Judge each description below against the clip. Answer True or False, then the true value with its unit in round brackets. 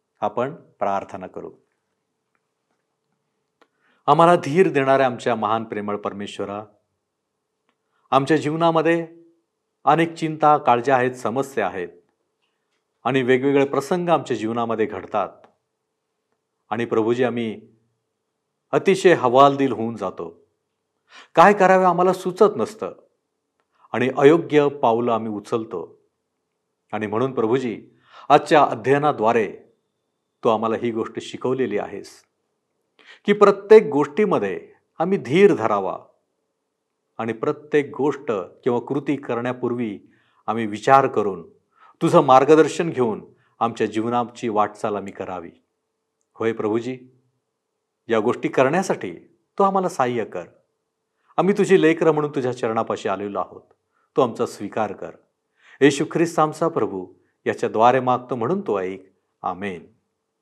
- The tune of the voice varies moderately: False (6.5 semitones)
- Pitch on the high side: False (135 Hz)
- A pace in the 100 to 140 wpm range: True (105 wpm)